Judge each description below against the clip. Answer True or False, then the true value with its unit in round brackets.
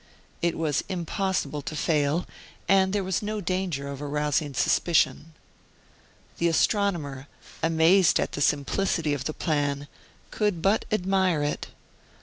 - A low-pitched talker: False (165 Hz)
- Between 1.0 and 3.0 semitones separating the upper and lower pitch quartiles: False (4.4 semitones)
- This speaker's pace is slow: True (130 wpm)